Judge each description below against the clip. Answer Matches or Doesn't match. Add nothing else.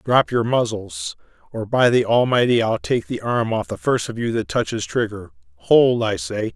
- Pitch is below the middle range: Matches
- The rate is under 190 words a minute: Doesn't match